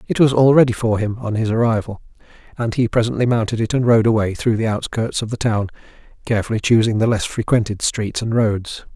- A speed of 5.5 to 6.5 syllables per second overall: Yes, 5.9 syllables/s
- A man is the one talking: Yes, male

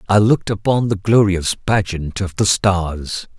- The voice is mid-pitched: No, low, 100 Hz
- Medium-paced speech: Yes, average, 160 wpm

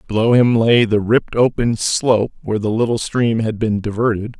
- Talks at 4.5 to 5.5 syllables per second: Yes, 5.4 syllables/s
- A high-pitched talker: No, low, 110 Hz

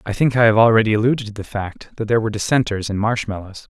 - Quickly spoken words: Yes, fast, 240 wpm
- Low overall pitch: Yes, low, 110 Hz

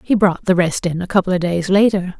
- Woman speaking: Yes, female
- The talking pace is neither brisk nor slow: No, fast, 275 wpm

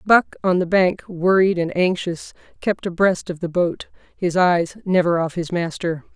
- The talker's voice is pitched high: No, medium, 175 Hz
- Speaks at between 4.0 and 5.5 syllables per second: Yes, 4.3 syllables/s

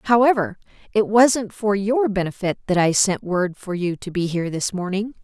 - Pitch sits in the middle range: No, high, 200 Hz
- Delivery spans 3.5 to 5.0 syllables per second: Yes, 4.9 syllables/s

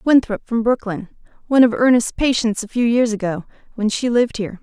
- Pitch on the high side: Yes, high, 230 Hz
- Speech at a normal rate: Yes, average, 195 wpm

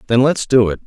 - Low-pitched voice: Yes, low, 125 Hz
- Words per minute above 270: Yes, fast, 280 wpm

